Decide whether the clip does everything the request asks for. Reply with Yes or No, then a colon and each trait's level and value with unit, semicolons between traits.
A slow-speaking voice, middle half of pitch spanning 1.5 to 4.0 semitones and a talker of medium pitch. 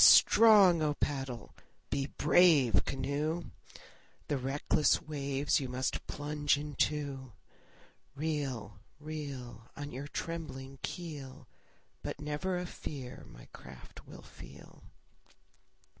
Yes: slow, 105 wpm; narrow, 2.5 semitones; medium, 145 Hz